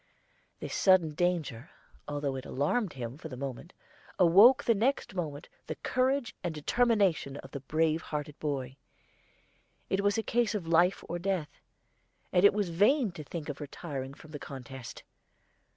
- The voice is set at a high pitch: No, medium, 165 Hz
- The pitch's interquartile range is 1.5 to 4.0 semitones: No, wide, 5.6 semitones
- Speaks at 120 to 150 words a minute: No, average, 160 wpm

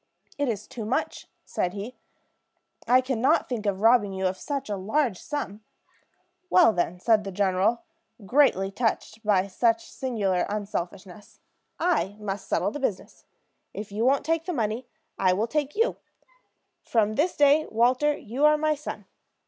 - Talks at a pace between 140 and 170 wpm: Yes, average, 160 wpm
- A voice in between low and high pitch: No, high, 225 Hz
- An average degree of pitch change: No, wide, 5.8 semitones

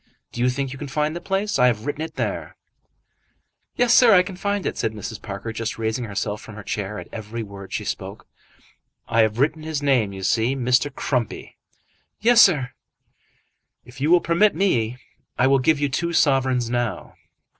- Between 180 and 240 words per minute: Yes, average, 190 wpm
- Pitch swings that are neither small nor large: No, wide, 5.9 semitones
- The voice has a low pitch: Yes, low, 130 Hz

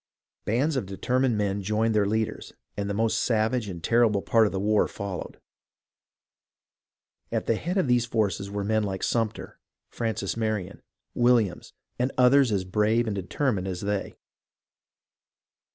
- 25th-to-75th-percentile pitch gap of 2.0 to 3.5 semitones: Yes, average, 2.9 semitones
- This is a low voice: Yes, low, 110 Hz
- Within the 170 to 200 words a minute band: No, average, 150 wpm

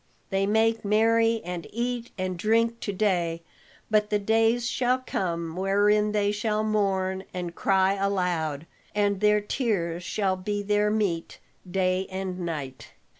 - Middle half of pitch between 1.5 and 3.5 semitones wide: Yes, average, 2.8 semitones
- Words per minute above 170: No, average, 140 wpm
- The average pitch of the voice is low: No, high, 200 Hz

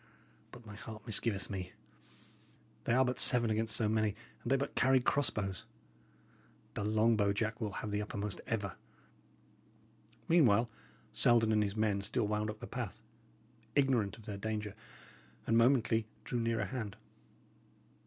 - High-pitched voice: No, low, 110 Hz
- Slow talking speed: No, average, 155 wpm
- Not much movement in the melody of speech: Yes, narrow, 2.1 semitones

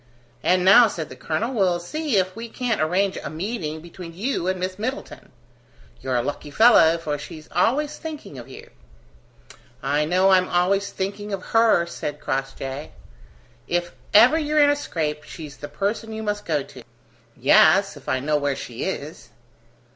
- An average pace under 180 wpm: Yes, average, 170 wpm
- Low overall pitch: No, medium, 180 Hz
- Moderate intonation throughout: No, wide, 6.2 semitones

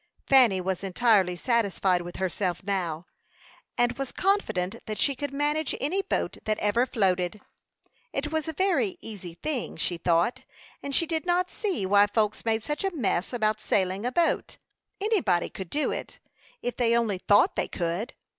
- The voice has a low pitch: No, high, 220 Hz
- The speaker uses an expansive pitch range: Yes, wide, 7.6 semitones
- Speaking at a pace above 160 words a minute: Yes, average, 170 wpm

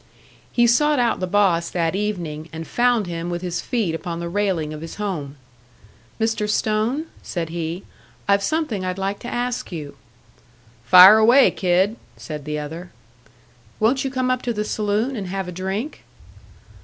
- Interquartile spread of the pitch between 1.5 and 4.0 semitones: No, average, 4.9 semitones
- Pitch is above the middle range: Yes, high, 195 Hz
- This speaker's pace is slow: No, average, 170 wpm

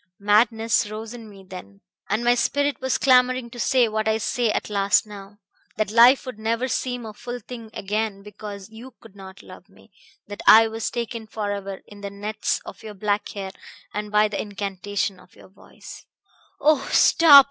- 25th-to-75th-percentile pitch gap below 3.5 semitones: Yes, average, 2.8 semitones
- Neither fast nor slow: Yes, average, 190 wpm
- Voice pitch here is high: Yes, high, 215 Hz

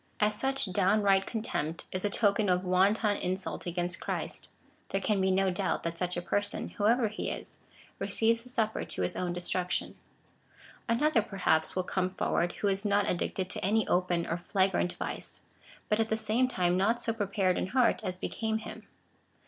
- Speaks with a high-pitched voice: Yes, high, 195 Hz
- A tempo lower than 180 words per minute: No, average, 185 wpm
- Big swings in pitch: No, average, 3.2 semitones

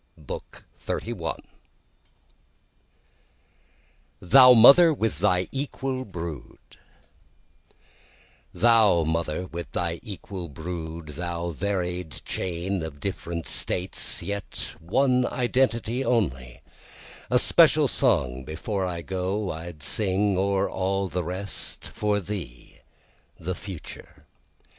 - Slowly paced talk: Yes, slow, 100 wpm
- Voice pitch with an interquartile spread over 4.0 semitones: No, average, 3.7 semitones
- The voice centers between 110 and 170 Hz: No, very low, 90 Hz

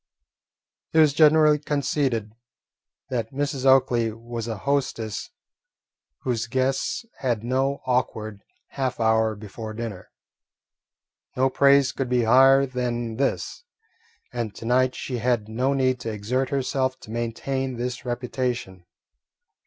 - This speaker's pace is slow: Yes, slow, 120 wpm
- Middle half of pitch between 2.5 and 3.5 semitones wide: Yes, average, 2.8 semitones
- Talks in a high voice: No, low, 125 Hz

